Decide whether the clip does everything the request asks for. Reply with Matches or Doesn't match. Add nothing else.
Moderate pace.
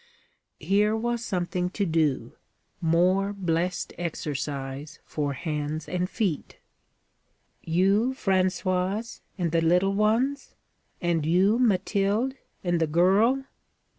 Doesn't match